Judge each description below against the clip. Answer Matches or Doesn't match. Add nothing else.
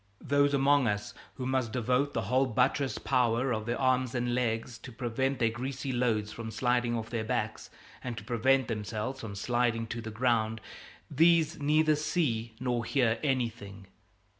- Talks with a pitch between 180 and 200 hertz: Doesn't match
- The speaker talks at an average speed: Matches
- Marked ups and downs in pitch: Doesn't match